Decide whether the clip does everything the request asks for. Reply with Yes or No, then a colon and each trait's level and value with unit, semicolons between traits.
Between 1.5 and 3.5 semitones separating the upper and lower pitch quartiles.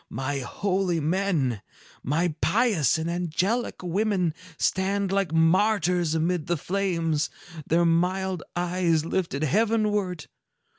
Yes: average, 3.2 semitones